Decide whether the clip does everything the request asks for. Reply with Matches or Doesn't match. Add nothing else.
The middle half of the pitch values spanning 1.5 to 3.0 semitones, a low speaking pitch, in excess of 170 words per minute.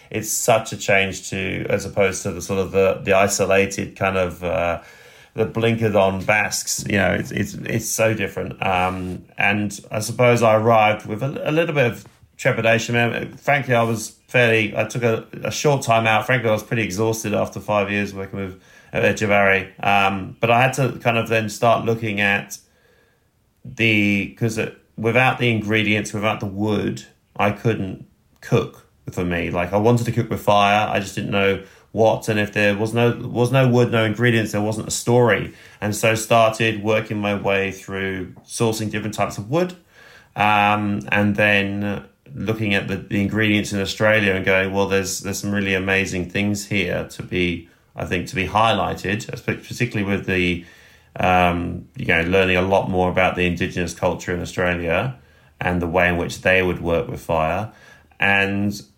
Matches